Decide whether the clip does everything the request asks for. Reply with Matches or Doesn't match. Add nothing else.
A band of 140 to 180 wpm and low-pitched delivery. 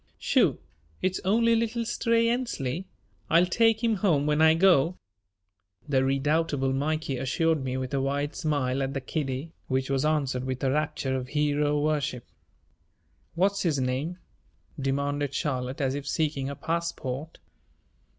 Doesn't match